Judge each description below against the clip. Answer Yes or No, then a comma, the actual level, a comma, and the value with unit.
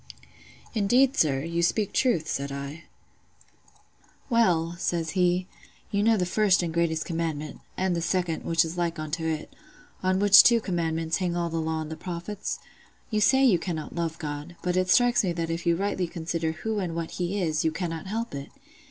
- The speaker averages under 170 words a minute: No, average, 185 wpm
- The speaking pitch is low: No, medium, 170 Hz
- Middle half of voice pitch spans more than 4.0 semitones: No, average, 3.0 semitones